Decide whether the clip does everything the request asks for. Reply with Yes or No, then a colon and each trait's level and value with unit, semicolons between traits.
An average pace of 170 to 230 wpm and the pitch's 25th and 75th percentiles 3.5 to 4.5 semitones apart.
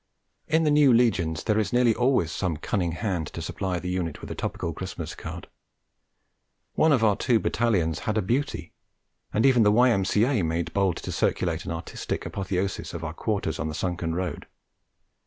No: average, 180 wpm; wide, 5.6 semitones